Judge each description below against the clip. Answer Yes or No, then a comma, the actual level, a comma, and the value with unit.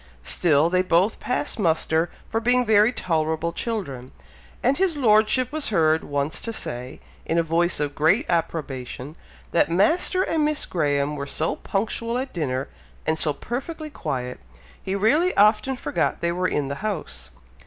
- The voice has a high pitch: No, medium, 175 Hz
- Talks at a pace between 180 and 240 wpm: No, average, 160 wpm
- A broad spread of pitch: Yes, wide, 7.1 semitones